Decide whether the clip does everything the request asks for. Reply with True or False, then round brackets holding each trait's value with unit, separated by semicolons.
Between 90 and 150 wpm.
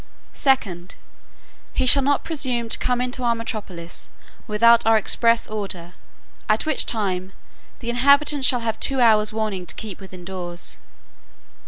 True (145 wpm)